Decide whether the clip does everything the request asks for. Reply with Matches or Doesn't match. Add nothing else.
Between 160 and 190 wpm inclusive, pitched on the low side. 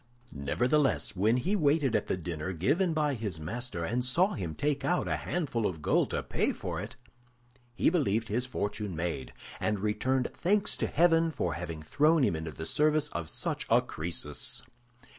Matches